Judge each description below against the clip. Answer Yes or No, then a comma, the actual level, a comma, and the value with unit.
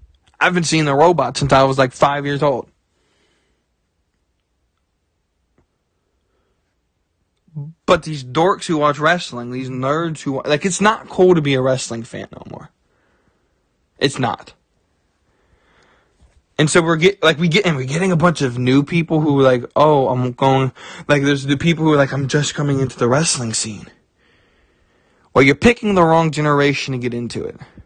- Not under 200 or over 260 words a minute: No, average, 170 wpm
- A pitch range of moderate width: Yes, average, 4.8 semitones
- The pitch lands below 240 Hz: Yes, medium, 140 Hz